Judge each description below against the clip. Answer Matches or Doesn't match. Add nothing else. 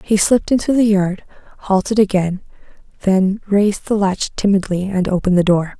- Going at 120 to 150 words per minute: Doesn't match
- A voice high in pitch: Matches